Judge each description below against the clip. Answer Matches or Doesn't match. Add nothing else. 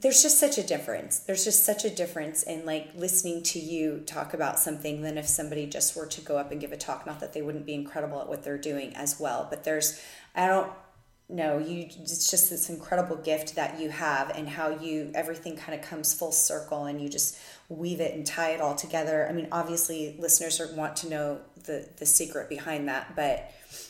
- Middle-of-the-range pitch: Matches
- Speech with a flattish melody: Matches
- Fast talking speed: Matches